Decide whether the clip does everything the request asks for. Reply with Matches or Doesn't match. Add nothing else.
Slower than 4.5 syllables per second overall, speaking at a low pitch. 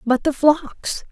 Doesn't match